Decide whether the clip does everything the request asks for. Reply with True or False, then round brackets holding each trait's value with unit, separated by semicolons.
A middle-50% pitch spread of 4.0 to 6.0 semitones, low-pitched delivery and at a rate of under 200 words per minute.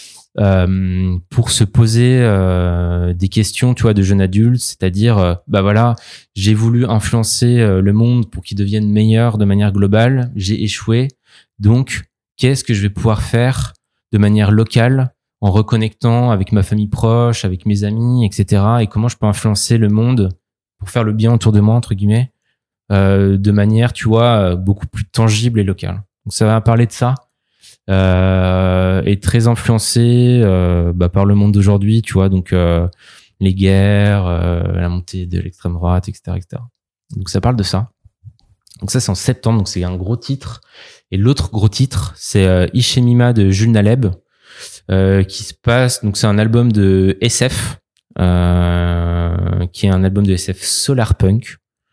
False (3.6 semitones; 105 Hz; 175 wpm)